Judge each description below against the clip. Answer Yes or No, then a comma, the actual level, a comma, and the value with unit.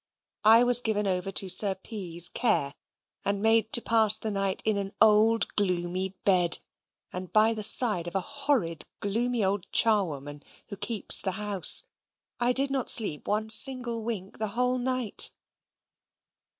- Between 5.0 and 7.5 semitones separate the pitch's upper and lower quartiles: No, average, 3.3 semitones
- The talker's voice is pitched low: No, high, 210 Hz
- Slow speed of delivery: No, average, 155 wpm